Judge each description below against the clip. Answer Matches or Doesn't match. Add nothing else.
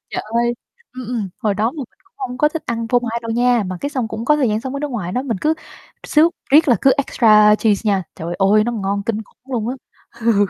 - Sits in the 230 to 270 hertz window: Matches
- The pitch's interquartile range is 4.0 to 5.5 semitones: Doesn't match